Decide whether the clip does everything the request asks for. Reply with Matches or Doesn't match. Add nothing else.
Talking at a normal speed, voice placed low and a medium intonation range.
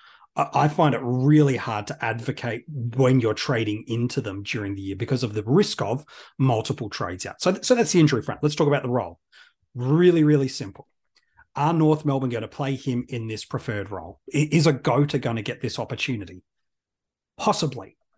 Matches